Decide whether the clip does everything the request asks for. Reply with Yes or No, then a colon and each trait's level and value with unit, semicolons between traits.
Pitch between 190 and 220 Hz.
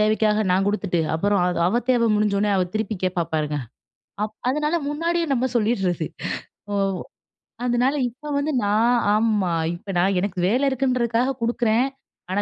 Yes: high, 215 Hz